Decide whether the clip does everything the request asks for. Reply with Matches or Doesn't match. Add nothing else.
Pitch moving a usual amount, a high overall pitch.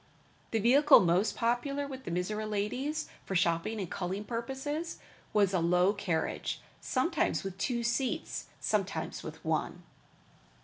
Doesn't match